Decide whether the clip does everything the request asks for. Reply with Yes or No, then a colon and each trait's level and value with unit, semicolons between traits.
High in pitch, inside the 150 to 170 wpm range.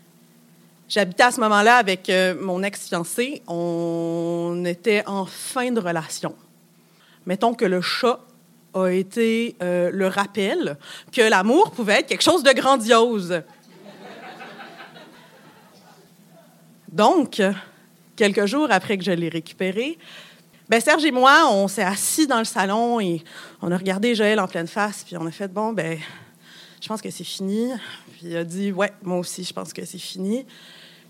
Yes: high, 195 Hz; average, 155 wpm